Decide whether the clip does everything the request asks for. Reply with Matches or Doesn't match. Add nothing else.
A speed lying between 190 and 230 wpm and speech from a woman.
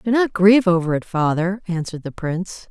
Matches